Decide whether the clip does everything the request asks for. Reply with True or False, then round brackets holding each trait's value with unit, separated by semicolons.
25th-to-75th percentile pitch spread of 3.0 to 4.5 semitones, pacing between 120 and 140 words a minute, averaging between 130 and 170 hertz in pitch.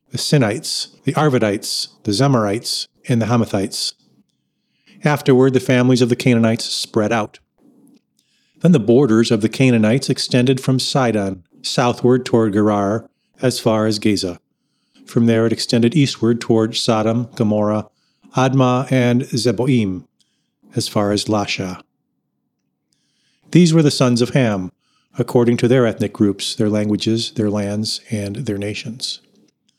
False (3.3 semitones; 135 wpm; 115 Hz)